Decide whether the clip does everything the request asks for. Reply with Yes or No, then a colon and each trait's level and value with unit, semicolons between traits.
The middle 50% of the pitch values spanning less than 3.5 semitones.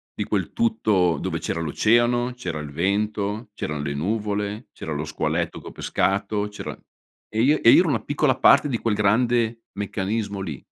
No: average, 4.7 semitones